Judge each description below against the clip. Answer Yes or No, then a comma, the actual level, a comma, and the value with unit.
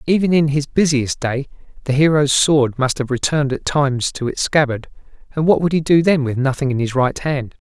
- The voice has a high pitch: No, medium, 140 Hz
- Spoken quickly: Yes, fast, 220 wpm